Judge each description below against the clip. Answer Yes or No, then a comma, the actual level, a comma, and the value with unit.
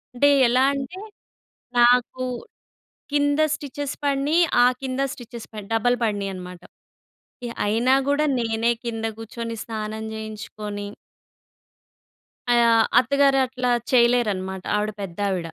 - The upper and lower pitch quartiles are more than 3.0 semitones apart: Yes, average, 3.5 semitones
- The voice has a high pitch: Yes, high, 235 Hz